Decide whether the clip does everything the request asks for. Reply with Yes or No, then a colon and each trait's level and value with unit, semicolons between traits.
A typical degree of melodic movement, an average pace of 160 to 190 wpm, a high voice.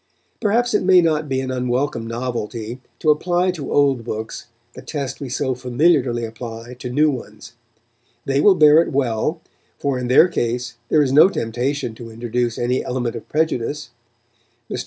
No: average, 4.1 semitones; average, 170 wpm; low, 130 Hz